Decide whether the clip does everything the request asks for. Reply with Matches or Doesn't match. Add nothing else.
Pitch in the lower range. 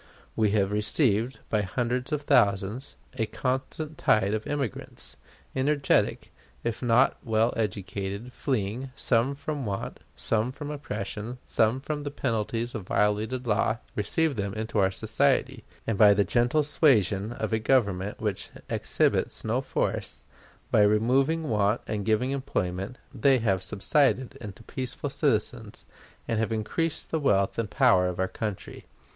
Matches